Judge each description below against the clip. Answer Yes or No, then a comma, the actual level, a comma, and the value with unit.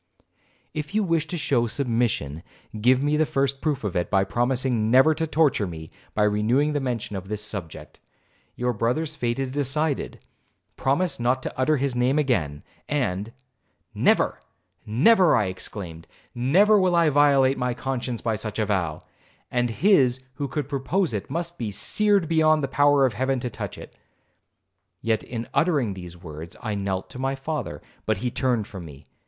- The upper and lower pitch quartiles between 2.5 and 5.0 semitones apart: No, wide, 5.6 semitones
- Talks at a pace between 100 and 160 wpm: No, average, 170 wpm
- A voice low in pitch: Yes, low, 125 Hz